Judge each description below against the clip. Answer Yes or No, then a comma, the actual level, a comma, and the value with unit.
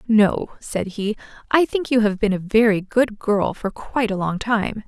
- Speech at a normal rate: No, fast, 210 wpm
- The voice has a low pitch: No, high, 215 Hz